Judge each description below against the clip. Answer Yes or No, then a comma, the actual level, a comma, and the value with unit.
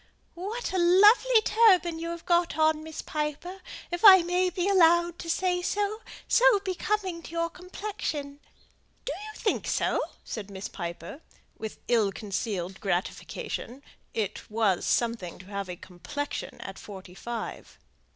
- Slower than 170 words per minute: Yes, average, 145 wpm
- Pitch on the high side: Yes, very high, 330 Hz